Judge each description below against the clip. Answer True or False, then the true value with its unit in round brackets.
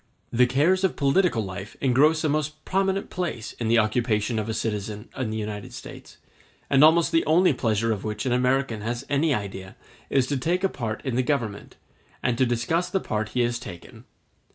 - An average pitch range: False (5.8 semitones)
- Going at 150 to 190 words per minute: False (200 wpm)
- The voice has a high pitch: False (125 Hz)